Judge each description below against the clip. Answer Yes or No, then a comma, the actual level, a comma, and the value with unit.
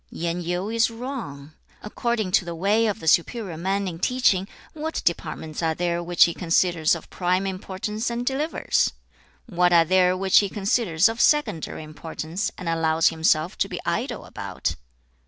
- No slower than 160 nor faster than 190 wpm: Yes, average, 165 wpm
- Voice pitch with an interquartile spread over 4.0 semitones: Yes, average, 4.6 semitones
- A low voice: No, medium, 185 Hz